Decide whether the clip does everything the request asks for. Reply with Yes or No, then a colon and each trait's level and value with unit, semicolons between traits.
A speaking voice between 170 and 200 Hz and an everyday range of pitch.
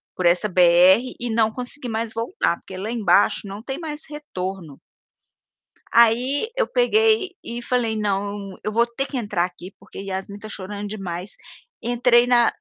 No: high, 220 Hz; average, 4.2 semitones